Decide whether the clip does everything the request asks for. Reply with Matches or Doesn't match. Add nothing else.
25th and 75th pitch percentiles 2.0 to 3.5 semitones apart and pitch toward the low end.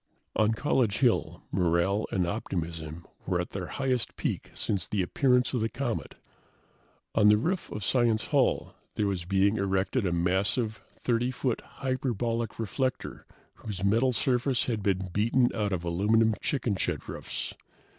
Doesn't match